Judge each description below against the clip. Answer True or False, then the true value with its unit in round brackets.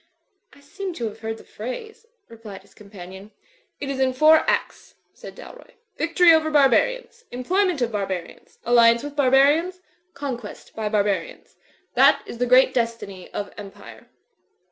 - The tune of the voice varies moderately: False (6.6 semitones)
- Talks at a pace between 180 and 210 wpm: False (150 wpm)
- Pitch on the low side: False (255 Hz)